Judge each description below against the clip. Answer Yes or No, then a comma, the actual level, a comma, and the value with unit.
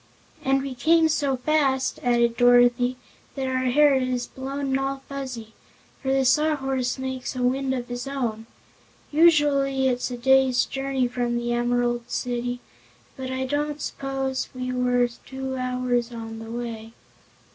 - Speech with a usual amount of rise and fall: No, narrow, 1.8 semitones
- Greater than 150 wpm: No, average, 145 wpm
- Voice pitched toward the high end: Yes, very high, 255 Hz